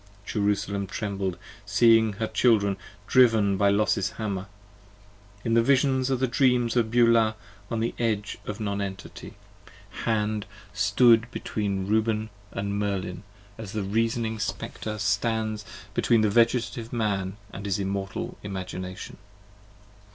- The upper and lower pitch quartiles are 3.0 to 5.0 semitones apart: No, narrow, 2.4 semitones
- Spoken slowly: Yes, slow, 130 wpm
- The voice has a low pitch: Yes, low, 105 Hz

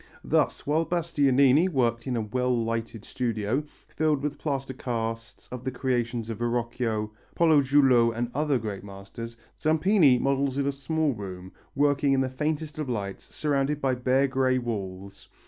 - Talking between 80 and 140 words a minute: No, average, 155 wpm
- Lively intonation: No, average, 3.7 semitones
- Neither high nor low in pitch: No, low, 130 Hz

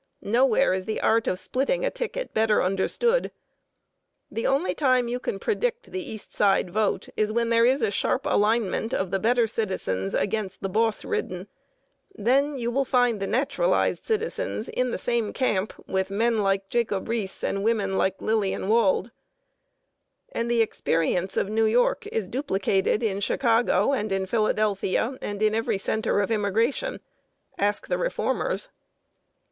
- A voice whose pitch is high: Yes, high, 225 Hz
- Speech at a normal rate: Yes, average, 160 wpm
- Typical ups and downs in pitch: Yes, average, 4.1 semitones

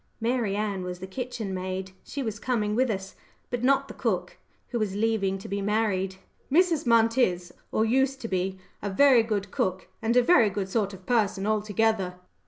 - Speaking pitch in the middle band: No, high, 215 Hz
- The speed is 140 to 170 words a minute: No, average, 190 wpm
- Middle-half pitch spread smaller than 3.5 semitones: No, average, 3.8 semitones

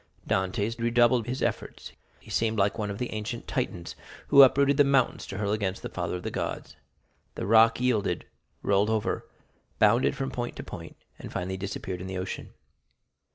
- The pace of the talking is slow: No, average, 180 wpm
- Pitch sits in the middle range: No, low, 110 Hz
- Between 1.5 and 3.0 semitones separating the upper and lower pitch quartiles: No, average, 3.6 semitones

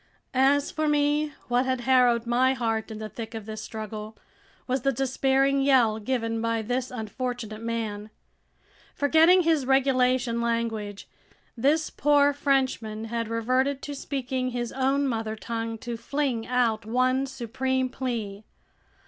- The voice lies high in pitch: Yes, very high, 250 Hz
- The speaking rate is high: No, average, 140 wpm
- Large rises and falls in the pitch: No, average, 3.1 semitones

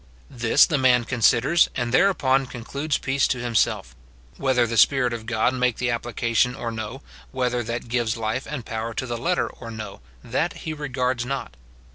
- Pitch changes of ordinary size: No, narrow, 2.3 semitones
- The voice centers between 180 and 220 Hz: No, low, 125 Hz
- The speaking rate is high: No, average, 175 wpm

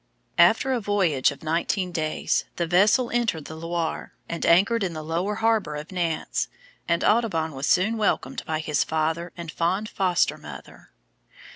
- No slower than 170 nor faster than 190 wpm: No, average, 160 wpm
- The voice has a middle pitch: Yes, medium, 170 Hz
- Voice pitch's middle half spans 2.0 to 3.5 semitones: No, average, 4.4 semitones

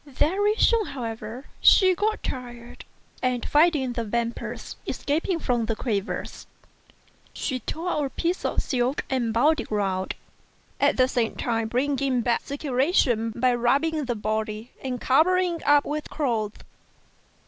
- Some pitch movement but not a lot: Yes, average, 4.5 semitones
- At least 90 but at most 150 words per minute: Yes, average, 145 wpm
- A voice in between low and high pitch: No, very high, 255 Hz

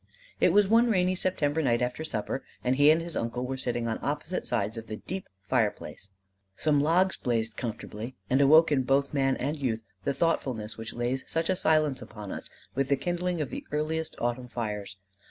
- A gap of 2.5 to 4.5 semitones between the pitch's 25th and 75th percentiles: No, average, 5.2 semitones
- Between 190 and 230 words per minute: Yes, average, 195 wpm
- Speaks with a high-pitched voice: No, low, 135 Hz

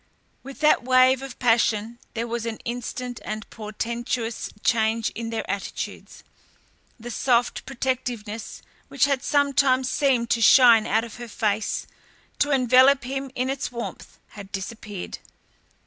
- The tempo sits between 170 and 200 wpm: No, slow, 135 wpm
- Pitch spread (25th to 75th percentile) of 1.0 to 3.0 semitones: Yes, narrow, 2.5 semitones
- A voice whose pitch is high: Yes, high, 240 Hz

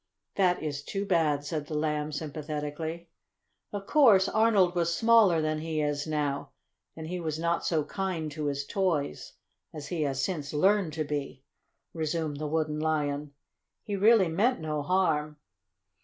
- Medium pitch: Yes, medium, 155 Hz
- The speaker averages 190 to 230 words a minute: No, average, 155 wpm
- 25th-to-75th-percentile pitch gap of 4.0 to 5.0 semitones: No, average, 3.4 semitones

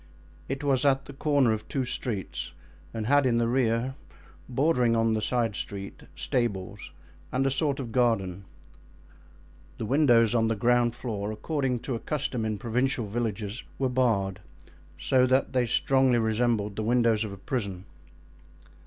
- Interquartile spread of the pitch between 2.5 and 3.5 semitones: Yes, average, 3.2 semitones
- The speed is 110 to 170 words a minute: Yes, average, 155 wpm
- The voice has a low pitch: Yes, low, 120 Hz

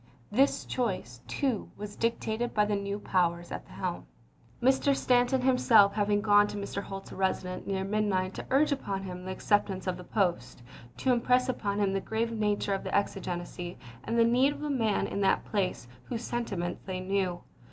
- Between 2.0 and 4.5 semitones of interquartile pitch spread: Yes, average, 3.8 semitones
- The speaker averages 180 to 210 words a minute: Yes, average, 195 wpm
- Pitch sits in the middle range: No, high, 205 Hz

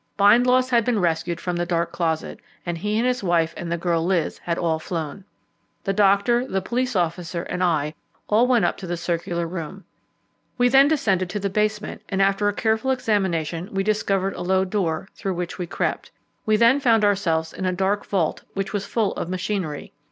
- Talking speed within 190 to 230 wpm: Yes, average, 200 wpm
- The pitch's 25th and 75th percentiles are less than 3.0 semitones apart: No, average, 3.7 semitones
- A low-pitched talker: No, high, 190 Hz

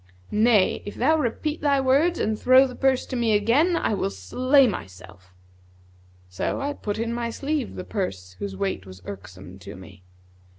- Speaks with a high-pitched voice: Yes, high, 220 Hz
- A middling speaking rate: Yes, average, 175 wpm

